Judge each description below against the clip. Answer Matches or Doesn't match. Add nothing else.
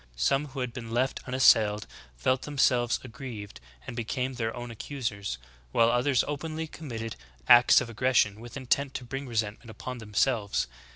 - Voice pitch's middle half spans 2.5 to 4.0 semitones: Matches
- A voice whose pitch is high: Doesn't match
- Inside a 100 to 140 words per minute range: Doesn't match